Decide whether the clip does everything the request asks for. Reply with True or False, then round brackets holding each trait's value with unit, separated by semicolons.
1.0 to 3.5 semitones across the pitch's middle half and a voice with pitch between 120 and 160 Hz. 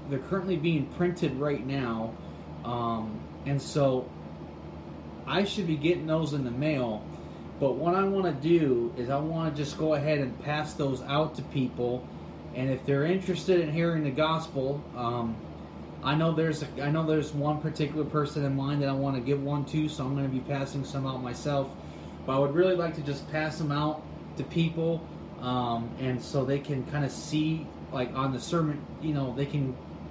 True (3.2 semitones; 140 Hz)